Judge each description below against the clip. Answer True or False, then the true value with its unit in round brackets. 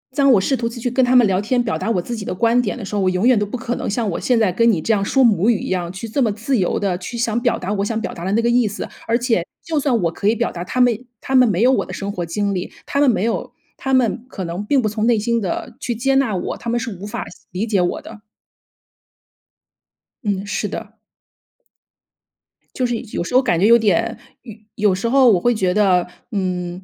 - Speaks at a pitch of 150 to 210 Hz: False (220 Hz)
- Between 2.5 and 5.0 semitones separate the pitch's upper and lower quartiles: True (3.8 semitones)